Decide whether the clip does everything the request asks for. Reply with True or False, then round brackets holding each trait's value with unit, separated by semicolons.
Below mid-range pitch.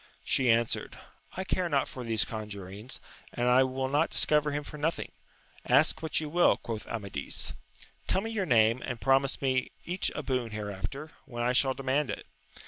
True (130 Hz)